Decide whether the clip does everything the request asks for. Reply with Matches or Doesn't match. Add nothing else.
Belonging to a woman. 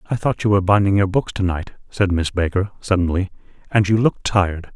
Doesn't match